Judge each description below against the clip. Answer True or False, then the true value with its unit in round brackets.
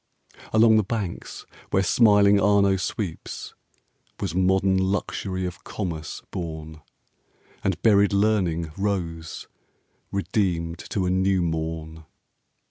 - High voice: False (95 Hz)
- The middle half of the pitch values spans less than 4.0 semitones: True (3.3 semitones)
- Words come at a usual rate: False (105 wpm)